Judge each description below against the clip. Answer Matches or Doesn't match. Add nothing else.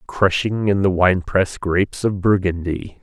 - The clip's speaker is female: Doesn't match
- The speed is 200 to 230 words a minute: Doesn't match